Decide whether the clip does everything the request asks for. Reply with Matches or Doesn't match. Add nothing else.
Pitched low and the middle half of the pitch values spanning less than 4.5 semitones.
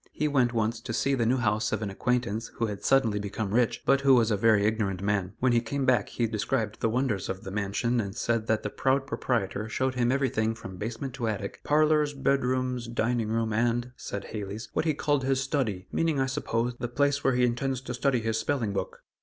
Matches